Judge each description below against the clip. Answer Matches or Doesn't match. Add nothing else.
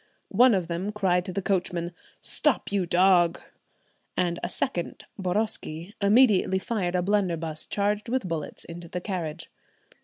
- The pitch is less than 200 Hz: Matches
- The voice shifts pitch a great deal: Doesn't match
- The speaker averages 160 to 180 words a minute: Doesn't match